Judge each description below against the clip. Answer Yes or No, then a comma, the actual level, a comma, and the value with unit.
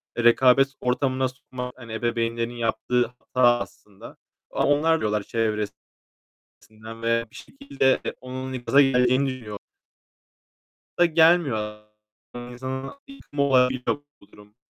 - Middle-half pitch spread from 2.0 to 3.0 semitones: Yes, narrow, 2.5 semitones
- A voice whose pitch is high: No, low, 125 Hz